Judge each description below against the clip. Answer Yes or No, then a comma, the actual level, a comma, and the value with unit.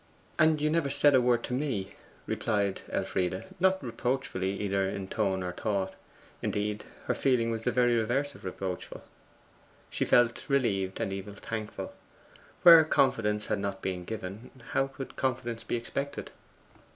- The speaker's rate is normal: Yes, average, 150 wpm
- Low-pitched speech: Yes, low, 115 Hz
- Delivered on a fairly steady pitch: No, average, 5.2 semitones